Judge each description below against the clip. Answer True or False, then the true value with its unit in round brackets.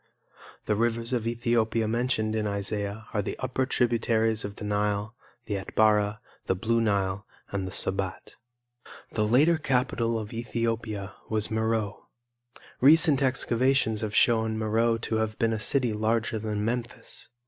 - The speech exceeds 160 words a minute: False (145 wpm)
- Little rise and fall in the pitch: True (1.9 semitones)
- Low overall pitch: True (110 Hz)